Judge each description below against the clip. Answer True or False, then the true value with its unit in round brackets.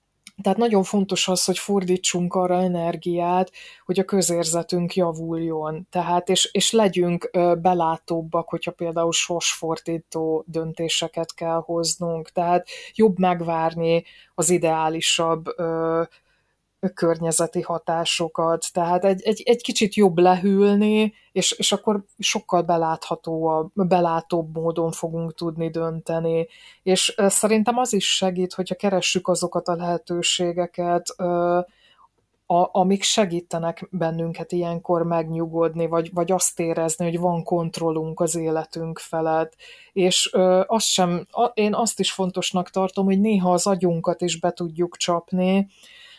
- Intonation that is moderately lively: False (2.1 semitones)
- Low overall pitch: False (175 Hz)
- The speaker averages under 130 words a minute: True (120 wpm)